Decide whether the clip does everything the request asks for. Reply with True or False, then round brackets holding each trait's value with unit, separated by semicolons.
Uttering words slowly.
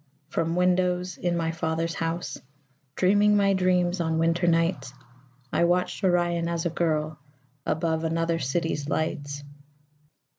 True (125 wpm)